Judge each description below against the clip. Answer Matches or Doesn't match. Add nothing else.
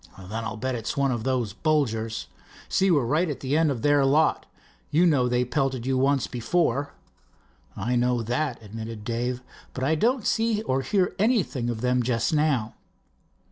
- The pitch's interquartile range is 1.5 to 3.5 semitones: Doesn't match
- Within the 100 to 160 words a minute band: Doesn't match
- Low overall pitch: Matches